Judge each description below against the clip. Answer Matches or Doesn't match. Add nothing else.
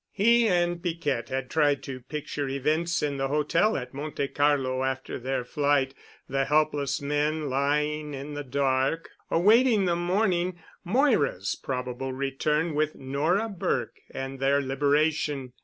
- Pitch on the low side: Doesn't match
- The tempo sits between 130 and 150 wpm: Matches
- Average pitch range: Matches